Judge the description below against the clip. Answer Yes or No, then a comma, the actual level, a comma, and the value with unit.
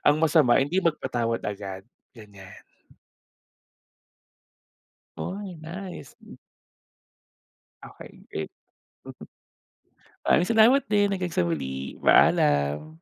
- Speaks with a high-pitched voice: No, low, 130 Hz